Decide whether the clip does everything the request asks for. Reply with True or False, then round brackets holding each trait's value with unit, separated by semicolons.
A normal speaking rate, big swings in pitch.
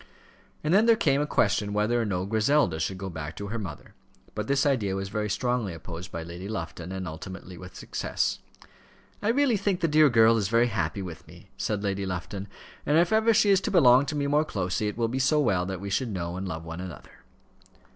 False (225 wpm; 7.2 semitones)